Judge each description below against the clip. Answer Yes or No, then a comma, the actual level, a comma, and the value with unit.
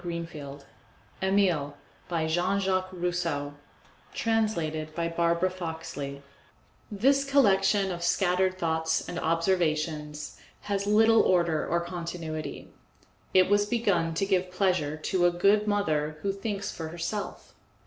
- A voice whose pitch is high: No, medium, 175 Hz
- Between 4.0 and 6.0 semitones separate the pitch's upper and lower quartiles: No, average, 3.5 semitones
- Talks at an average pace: No, slow, 125 wpm